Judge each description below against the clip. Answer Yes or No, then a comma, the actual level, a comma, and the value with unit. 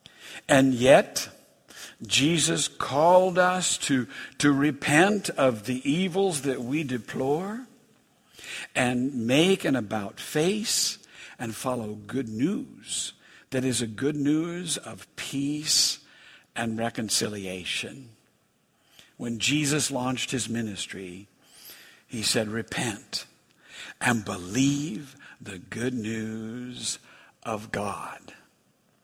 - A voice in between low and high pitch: No, low, 130 Hz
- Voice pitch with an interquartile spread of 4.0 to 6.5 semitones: Yes, average, 4.8 semitones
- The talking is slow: Yes, slow, 95 wpm